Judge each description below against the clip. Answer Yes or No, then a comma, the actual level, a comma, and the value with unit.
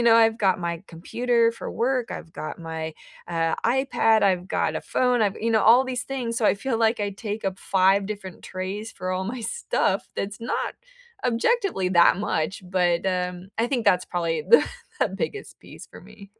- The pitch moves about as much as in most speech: Yes, average, 4.1 semitones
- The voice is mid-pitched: No, high, 205 Hz